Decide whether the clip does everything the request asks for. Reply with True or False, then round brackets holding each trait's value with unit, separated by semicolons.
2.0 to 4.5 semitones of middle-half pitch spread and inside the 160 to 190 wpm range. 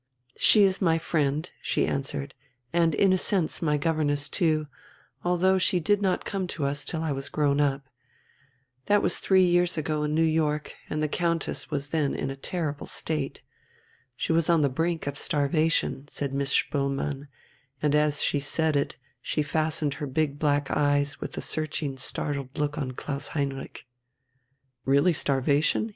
True (2.6 semitones; 170 wpm)